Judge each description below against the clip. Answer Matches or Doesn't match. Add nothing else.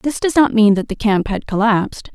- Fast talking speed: Matches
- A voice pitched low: Doesn't match